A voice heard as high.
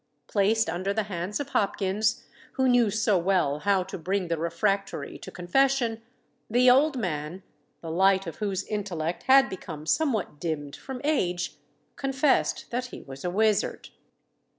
Yes: high, 195 Hz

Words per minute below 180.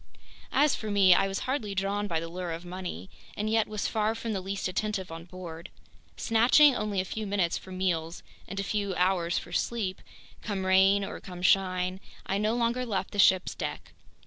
No: average, 200 wpm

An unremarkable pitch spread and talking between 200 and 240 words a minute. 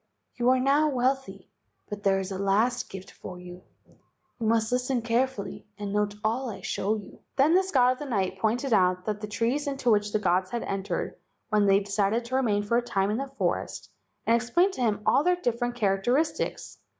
Yes: average, 4.1 semitones; fast, 205 wpm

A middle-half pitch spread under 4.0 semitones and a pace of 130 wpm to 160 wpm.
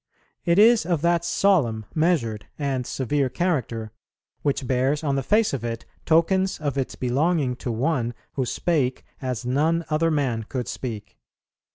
No: average, 5.1 semitones; average, 155 wpm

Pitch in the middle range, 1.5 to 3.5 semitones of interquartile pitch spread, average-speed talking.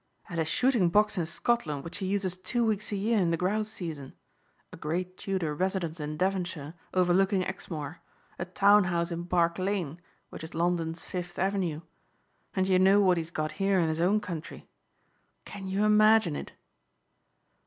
Yes: medium, 180 Hz; average, 2.9 semitones; average, 175 wpm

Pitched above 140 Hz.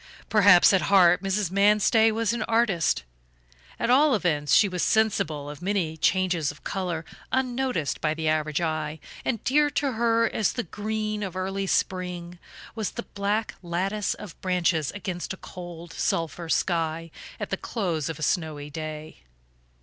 Yes: medium, 185 Hz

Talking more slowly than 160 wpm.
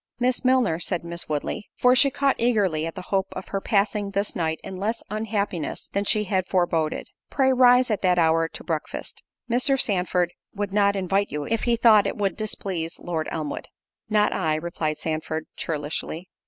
No: average, 180 wpm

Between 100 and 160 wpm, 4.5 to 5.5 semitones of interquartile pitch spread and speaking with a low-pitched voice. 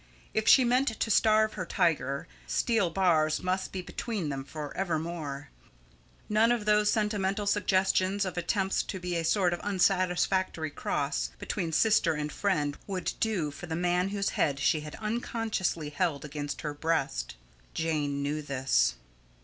No: average, 155 wpm; average, 5.1 semitones; medium, 180 Hz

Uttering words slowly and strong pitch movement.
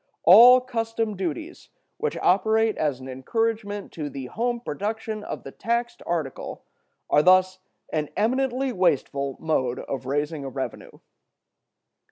Yes: slow, 130 wpm; wide, 7.7 semitones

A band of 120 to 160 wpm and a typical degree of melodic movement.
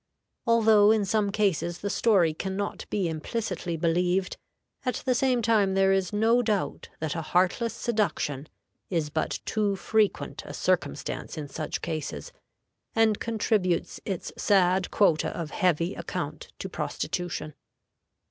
Yes: average, 140 wpm; average, 4.2 semitones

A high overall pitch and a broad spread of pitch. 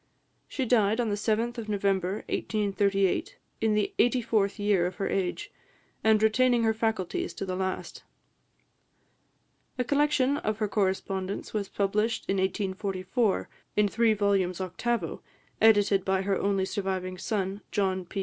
No: high, 205 Hz; narrow, 2.6 semitones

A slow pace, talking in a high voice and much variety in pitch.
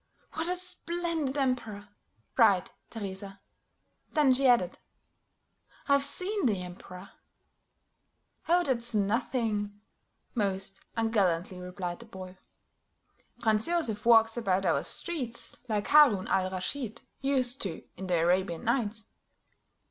Yes: slow, 110 wpm; high, 220 Hz; wide, 5.8 semitones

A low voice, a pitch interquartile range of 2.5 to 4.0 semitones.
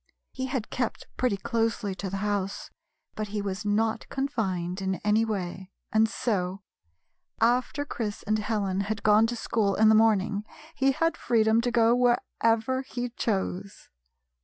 No: high, 220 Hz; average, 2.9 semitones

